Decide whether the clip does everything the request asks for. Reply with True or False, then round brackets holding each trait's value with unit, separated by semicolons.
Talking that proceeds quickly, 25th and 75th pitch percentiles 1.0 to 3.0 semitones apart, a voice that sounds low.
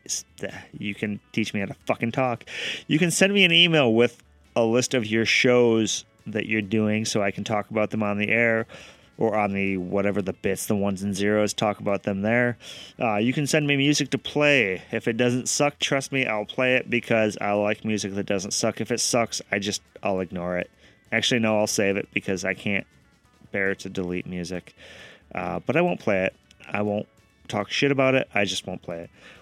False (220 wpm; 3.4 semitones; 105 Hz)